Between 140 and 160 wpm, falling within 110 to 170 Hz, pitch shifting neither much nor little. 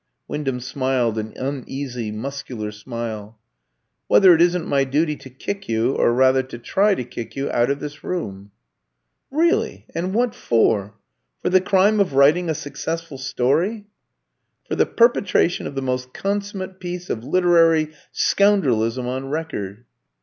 No: average, 150 wpm; medium, 140 Hz; wide, 6.5 semitones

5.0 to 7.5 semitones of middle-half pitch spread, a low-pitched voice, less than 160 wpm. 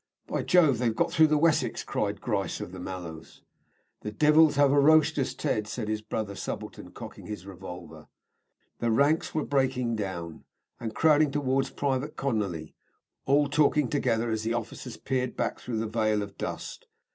No: average, 5.3 semitones; low, 120 Hz; average, 165 wpm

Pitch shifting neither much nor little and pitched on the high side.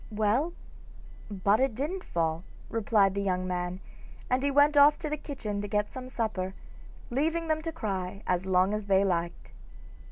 No: wide, 7.0 semitones; high, 210 Hz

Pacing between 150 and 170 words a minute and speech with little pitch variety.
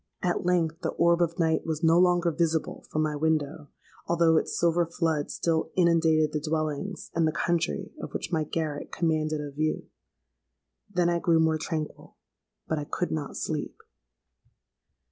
Yes: average, 160 wpm; narrow, 1.7 semitones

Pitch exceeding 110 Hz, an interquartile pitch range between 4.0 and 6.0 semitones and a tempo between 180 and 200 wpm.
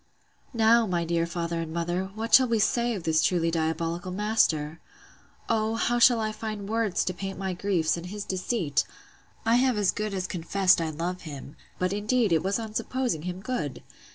Yes: high, 190 Hz; average, 4.7 semitones; average, 190 wpm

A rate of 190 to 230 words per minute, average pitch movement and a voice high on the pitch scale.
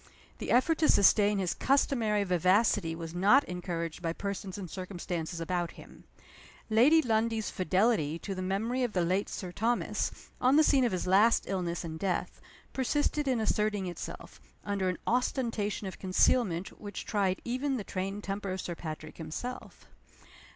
No: average, 160 wpm; average, 4.3 semitones; high, 200 Hz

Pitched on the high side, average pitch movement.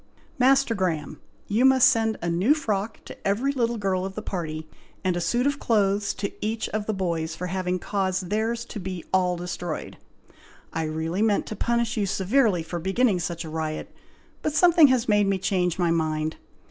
Yes: high, 195 Hz; average, 4.6 semitones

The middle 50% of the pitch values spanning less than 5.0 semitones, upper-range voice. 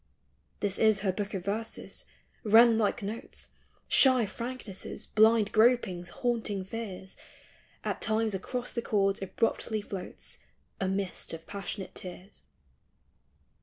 Yes: average, 2.8 semitones; high, 210 Hz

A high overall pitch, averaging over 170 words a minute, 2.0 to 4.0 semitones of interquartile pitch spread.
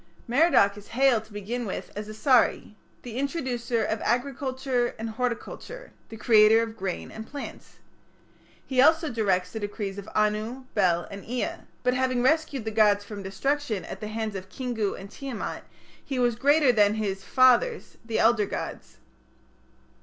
No: high, 225 Hz; average, 160 wpm; average, 3.6 semitones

